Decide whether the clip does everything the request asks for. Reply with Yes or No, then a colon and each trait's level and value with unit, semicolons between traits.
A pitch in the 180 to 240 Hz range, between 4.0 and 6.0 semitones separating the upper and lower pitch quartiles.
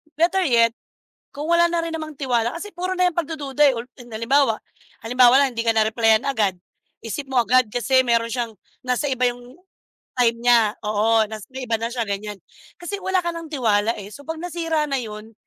No: very high, 250 Hz; average, 5.3 semitones